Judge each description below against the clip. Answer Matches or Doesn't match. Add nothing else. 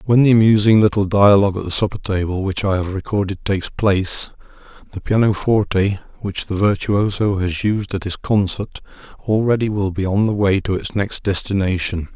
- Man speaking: Matches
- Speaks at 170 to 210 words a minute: Matches